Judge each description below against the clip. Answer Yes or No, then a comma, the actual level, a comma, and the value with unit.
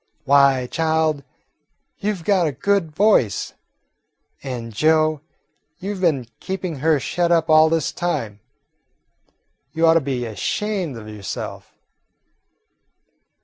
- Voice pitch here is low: No, medium, 155 Hz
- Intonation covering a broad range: No, average, 4.8 semitones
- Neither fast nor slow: No, slow, 120 wpm